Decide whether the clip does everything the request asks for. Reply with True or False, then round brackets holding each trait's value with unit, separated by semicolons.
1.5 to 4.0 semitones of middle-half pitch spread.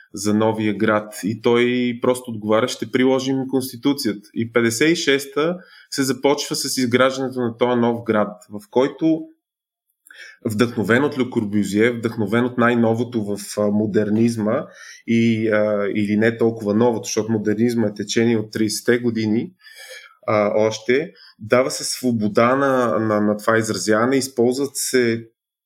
True (2.8 semitones)